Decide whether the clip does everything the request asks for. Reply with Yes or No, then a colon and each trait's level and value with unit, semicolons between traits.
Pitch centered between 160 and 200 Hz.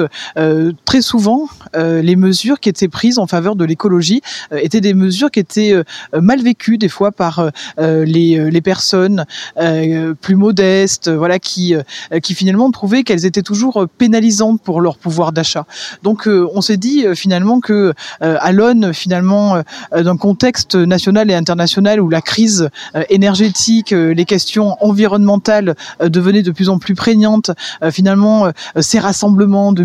Yes: high, 190 Hz